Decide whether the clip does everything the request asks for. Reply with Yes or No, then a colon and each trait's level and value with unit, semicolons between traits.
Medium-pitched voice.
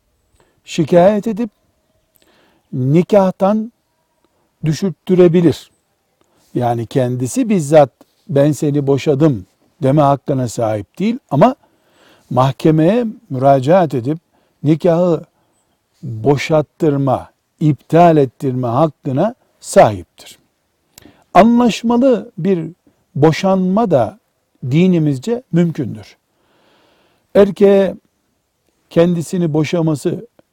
Yes: medium, 160 Hz